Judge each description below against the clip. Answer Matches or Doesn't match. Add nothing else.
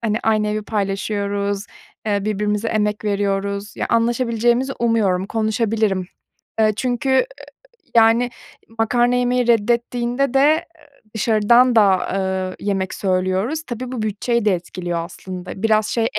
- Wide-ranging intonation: Doesn't match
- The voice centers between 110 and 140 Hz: Doesn't match